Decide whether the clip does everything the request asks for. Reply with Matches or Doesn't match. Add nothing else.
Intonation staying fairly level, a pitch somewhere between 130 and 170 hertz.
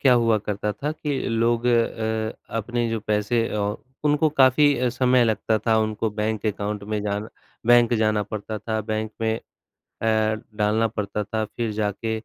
Doesn't match